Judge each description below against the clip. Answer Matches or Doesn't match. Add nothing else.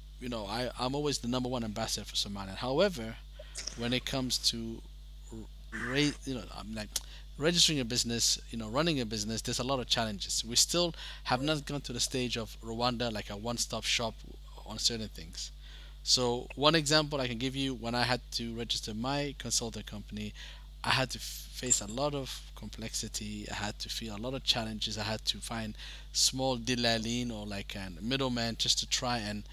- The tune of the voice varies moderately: Matches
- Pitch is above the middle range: Doesn't match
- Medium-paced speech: Matches